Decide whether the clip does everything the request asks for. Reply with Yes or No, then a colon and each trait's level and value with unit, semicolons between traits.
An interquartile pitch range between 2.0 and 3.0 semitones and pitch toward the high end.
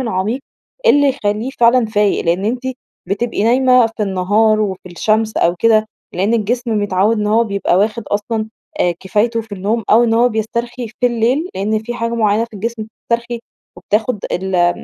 Yes: narrow, 2.4 semitones; high, 220 Hz